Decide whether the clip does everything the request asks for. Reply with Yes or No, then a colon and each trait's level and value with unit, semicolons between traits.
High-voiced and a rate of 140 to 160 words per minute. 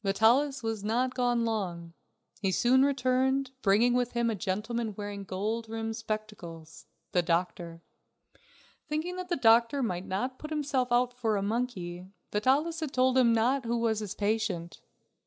Yes: high, 225 Hz; average, 155 wpm